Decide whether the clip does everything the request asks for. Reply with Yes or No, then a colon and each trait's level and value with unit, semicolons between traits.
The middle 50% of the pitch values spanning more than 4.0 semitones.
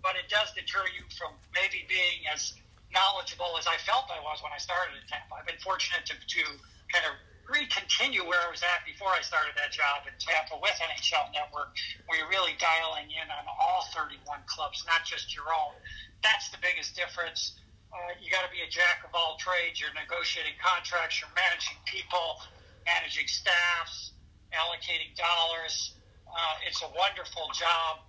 No: average, 3.1 semitones